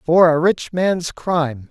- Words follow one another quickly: No, average, 175 wpm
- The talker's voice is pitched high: No, medium, 165 Hz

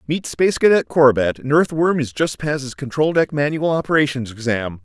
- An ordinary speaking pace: Yes, average, 175 wpm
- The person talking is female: No, male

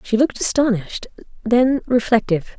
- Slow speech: Yes, slow, 115 wpm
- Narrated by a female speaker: Yes, female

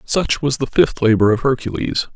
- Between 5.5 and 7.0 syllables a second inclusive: No, 5.0 syllables/s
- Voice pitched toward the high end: No, low, 115 Hz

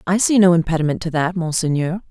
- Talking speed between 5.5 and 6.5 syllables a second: Yes, 6.3 syllables/s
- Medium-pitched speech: Yes, medium, 175 Hz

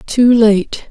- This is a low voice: No, high, 225 Hz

